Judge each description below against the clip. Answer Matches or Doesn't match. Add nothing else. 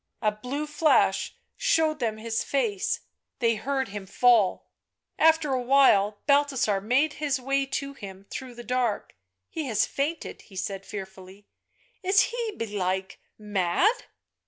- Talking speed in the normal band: Matches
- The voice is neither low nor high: Doesn't match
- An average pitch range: Doesn't match